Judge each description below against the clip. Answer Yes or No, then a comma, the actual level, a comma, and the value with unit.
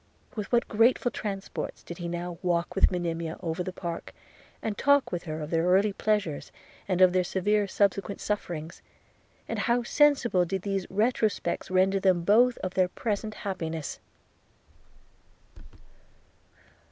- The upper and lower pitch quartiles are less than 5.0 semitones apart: Yes, average, 3.3 semitones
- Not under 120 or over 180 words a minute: Yes, average, 140 wpm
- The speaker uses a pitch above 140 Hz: Yes, high, 190 Hz